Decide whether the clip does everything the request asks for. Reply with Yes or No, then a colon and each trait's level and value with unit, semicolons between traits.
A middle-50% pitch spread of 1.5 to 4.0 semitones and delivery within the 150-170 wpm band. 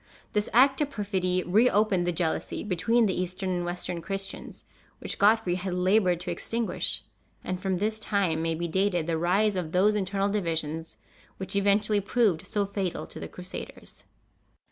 Yes: average, 2.9 semitones; average, 165 wpm